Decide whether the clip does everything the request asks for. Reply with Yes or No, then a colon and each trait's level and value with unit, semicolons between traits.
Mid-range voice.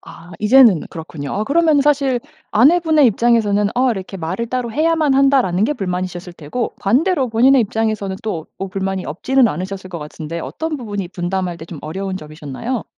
No: high, 205 Hz